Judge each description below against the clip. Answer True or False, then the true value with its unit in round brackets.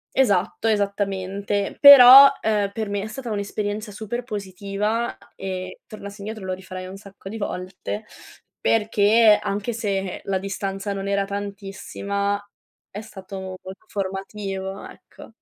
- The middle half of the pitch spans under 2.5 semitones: True (1.7 semitones)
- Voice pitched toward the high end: True (200 Hz)